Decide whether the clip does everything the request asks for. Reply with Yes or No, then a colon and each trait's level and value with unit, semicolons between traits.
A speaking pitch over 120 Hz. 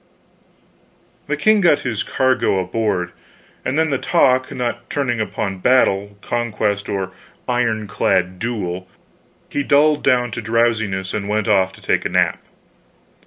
No: low, 115 Hz